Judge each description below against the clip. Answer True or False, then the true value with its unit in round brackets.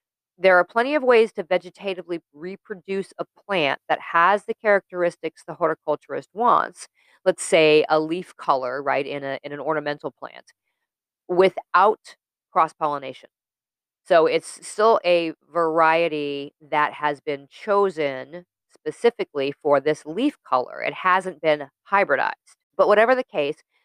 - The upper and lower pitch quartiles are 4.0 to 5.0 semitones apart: True (4.6 semitones)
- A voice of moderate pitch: True (170 Hz)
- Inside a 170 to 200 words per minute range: False (135 wpm)